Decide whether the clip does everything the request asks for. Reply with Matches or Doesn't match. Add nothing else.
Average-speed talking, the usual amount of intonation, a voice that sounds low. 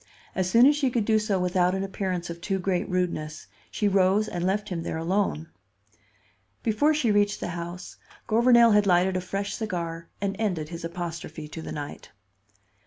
Doesn't match